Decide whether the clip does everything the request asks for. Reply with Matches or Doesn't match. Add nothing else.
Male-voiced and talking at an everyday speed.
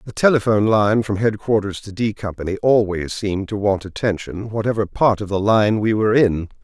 Matches